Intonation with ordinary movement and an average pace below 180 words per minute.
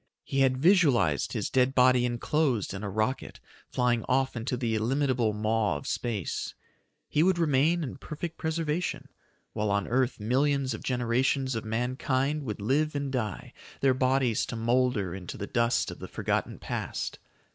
Yes: average, 3.6 semitones; average, 160 wpm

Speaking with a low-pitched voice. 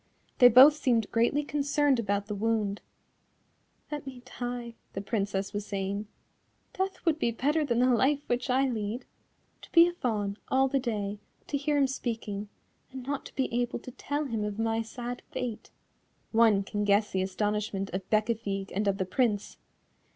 No: high, 230 Hz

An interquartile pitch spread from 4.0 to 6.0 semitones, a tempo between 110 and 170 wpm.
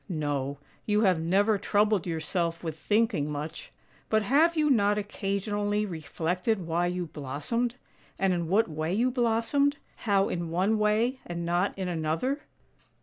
Yes: average, 4.8 semitones; average, 155 wpm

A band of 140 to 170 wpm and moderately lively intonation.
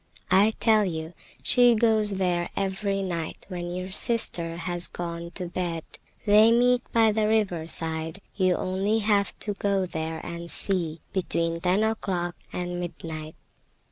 Yes: average, 145 wpm; average, 3.6 semitones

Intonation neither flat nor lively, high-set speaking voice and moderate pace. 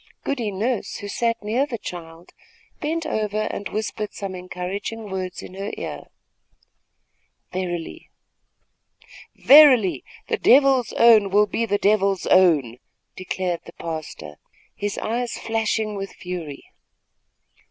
No: average, 3.9 semitones; high, 205 Hz; slow, 115 wpm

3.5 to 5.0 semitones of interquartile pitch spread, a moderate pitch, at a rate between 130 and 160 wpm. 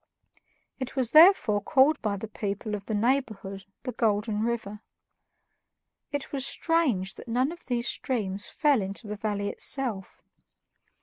No: average, 4.5 semitones; high, 225 Hz; average, 140 wpm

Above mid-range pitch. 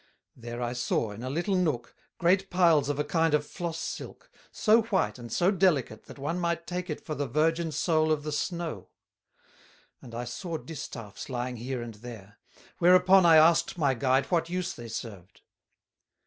No: medium, 155 Hz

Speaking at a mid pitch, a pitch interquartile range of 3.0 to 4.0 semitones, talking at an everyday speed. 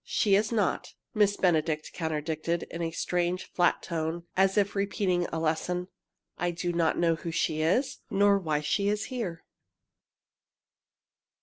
Yes: medium, 175 Hz; average, 3.4 semitones; average, 145 wpm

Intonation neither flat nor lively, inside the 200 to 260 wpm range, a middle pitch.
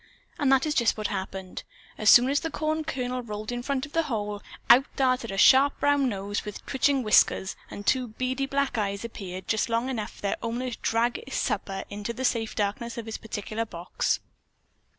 No: average, 4.1 semitones; fast, 205 wpm; high, 235 Hz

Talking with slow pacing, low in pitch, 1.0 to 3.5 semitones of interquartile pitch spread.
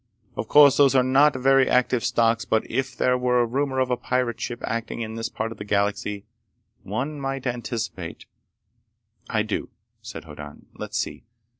No: average, 175 wpm; low, 125 Hz; average, 3.0 semitones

